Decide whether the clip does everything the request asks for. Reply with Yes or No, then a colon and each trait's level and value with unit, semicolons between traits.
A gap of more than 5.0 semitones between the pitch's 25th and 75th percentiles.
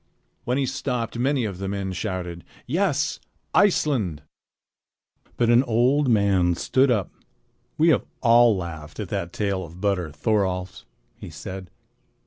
Yes: wide, 5.4 semitones